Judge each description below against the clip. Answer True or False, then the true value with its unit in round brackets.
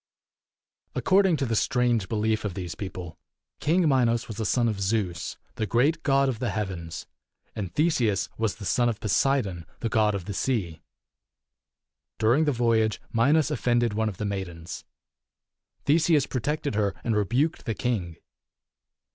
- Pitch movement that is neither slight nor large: True (4.8 semitones)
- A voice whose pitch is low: True (115 Hz)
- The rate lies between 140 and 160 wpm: True (155 wpm)